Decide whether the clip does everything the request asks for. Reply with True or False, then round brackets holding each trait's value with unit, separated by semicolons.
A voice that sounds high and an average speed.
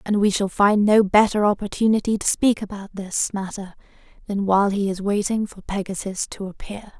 True (200 Hz; 180 wpm)